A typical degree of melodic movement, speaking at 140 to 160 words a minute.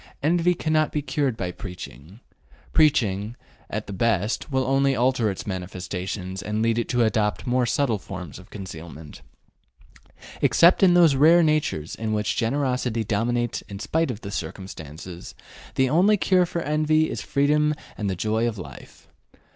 No: wide, 7.2 semitones; average, 155 wpm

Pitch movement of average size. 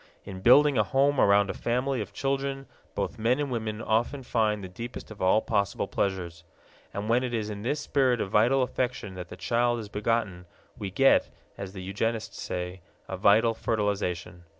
Yes: average, 4.1 semitones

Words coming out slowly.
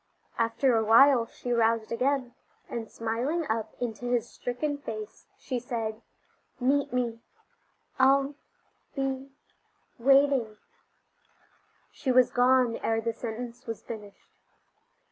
Yes: slow, 110 wpm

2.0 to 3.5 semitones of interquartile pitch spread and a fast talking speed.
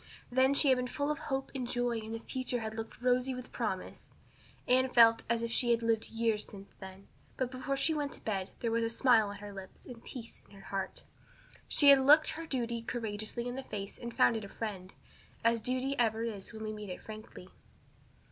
Yes: average, 2.8 semitones; fast, 225 wpm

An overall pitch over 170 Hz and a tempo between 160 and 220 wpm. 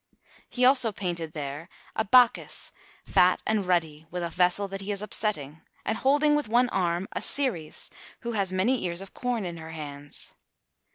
Yes: high, 190 Hz; average, 175 wpm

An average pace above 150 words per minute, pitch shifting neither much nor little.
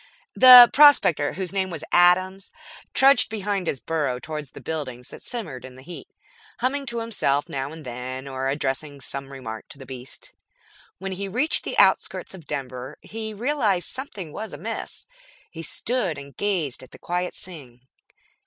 No: average, 165 wpm; wide, 7.3 semitones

